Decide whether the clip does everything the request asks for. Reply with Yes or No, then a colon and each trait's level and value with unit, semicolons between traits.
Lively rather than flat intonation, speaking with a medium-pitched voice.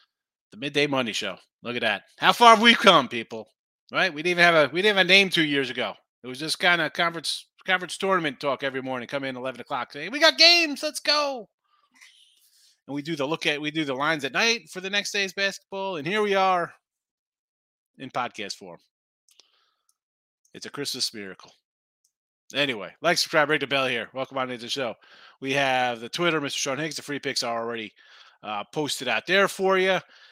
Yes: wide, 6.4 semitones; medium, 160 Hz